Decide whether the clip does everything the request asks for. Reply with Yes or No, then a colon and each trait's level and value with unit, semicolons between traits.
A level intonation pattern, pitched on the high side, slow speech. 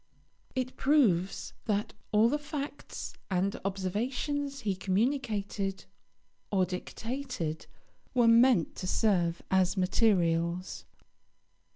No: wide, 5.5 semitones; high, 205 Hz; slow, 90 wpm